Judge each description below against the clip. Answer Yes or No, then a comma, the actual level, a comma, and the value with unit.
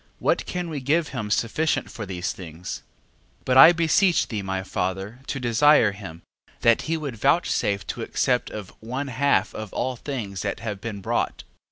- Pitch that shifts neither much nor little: No, wide, 6.1 semitones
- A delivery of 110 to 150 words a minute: No, average, 180 wpm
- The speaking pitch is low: Yes, low, 115 Hz